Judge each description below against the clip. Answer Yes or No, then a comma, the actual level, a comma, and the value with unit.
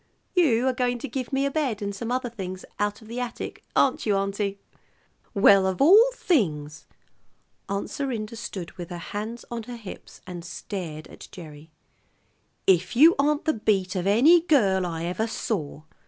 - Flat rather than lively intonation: No, average, 5.3 semitones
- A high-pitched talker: Yes, high, 210 Hz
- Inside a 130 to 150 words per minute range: No, average, 175 wpm